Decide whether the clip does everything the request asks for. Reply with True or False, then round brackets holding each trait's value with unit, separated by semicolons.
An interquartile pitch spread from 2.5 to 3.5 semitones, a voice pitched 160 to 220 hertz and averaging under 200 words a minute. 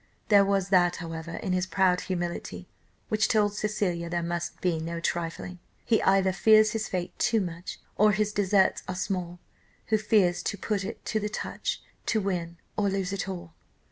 True (3.0 semitones; 190 Hz; 180 wpm)